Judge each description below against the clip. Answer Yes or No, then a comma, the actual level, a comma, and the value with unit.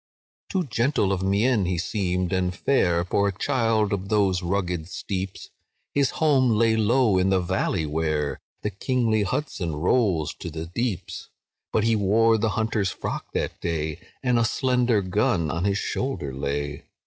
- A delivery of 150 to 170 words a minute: Yes, average, 160 wpm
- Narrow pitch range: No, average, 4.4 semitones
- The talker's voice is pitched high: No, low, 100 Hz